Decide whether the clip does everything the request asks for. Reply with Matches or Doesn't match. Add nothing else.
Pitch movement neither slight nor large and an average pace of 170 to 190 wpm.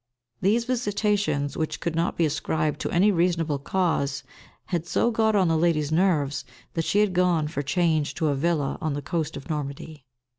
Matches